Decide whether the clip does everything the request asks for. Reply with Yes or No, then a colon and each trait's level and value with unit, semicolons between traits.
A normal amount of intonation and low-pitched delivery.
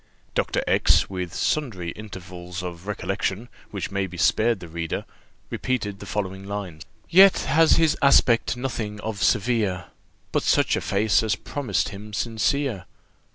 Yes: average, 4.4 semitones; low, 105 Hz